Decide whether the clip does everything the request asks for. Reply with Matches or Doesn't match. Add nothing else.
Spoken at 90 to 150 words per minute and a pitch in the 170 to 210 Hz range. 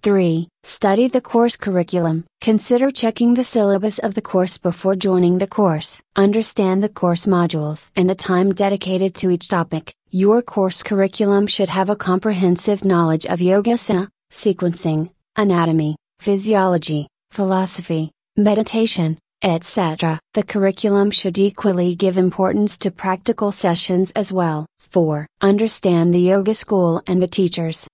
Matches